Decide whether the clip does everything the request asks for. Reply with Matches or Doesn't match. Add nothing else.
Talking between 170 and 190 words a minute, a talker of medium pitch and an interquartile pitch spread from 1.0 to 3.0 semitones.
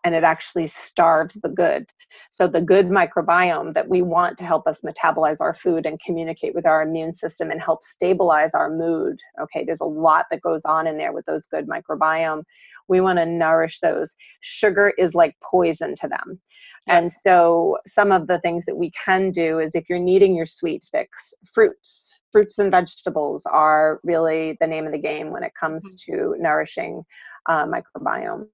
Matches